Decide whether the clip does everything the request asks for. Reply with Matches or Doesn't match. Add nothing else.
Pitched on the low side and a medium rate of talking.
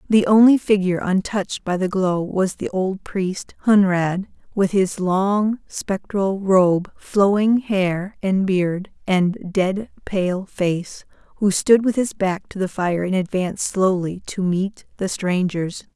Doesn't match